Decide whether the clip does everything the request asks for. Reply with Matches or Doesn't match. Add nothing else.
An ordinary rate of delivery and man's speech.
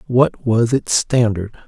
Matches